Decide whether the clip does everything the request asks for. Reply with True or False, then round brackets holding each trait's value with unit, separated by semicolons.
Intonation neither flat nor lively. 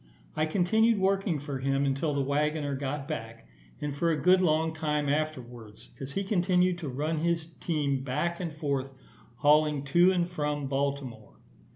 True (3.6 semitones)